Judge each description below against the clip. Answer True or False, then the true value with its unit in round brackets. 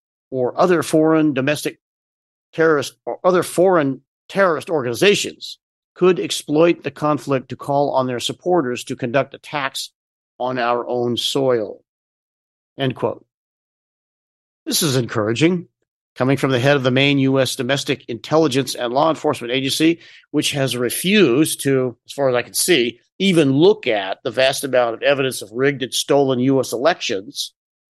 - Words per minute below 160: True (150 wpm)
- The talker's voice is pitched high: False (135 Hz)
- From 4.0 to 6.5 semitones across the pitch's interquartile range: False (3.5 semitones)